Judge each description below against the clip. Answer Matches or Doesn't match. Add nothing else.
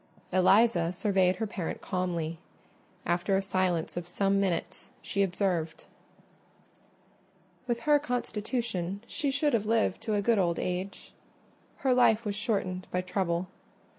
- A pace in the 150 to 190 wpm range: Doesn't match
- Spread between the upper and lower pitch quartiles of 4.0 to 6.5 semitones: Doesn't match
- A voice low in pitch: Doesn't match